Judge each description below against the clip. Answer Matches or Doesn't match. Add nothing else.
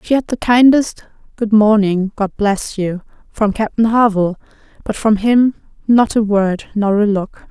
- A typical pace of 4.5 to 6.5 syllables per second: Doesn't match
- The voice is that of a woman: Matches